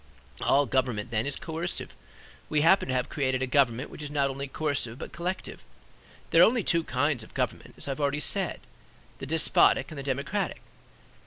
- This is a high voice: No, medium, 140 Hz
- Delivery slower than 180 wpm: No, average, 190 wpm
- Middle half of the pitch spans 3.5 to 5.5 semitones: No, average, 2.8 semitones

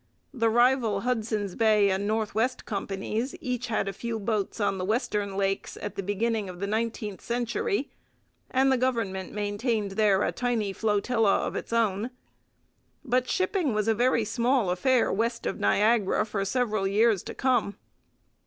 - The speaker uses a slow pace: No, average, 160 wpm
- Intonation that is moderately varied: Yes, average, 3.3 semitones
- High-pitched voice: Yes, high, 220 Hz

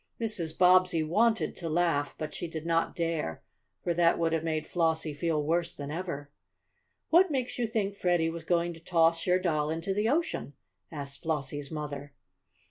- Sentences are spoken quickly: No, average, 175 wpm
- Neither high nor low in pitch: Yes, medium, 165 Hz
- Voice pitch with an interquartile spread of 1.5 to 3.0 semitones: Yes, narrow, 2.6 semitones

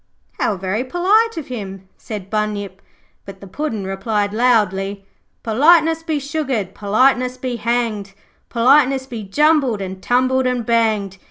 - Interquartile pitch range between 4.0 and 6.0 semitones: Yes, average, 4.8 semitones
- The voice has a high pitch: Yes, high, 230 Hz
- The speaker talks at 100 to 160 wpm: Yes, slow, 135 wpm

